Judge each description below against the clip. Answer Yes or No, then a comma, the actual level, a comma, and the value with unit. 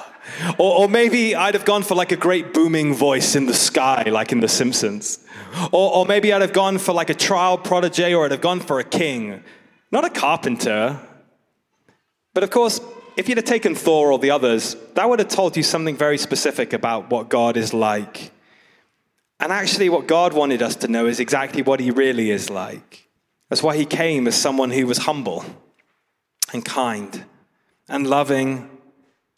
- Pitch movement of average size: No, wide, 5.8 semitones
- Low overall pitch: No, medium, 160 Hz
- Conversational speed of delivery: Yes, average, 190 wpm